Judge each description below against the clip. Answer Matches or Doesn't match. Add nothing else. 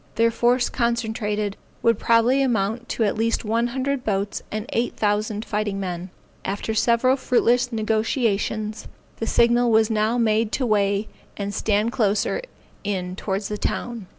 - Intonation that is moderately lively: Doesn't match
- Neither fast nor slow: Matches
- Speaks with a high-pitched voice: Matches